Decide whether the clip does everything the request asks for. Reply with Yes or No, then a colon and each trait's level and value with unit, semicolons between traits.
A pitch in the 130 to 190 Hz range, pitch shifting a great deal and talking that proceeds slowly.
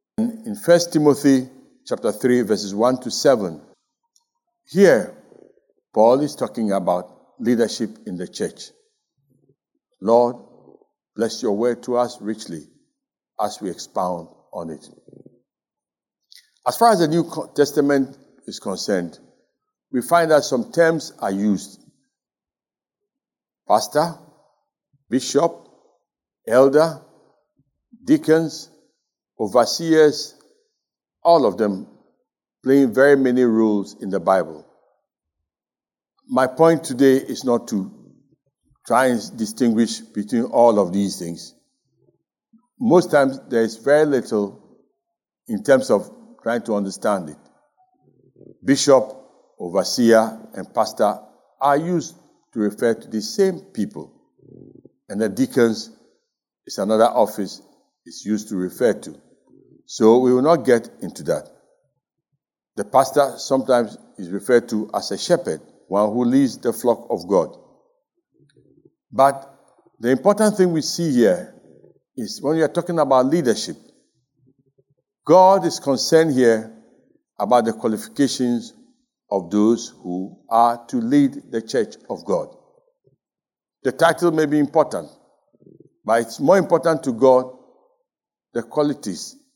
Yes: medium, 140 Hz; wide, 7.7 semitones; slow, 120 wpm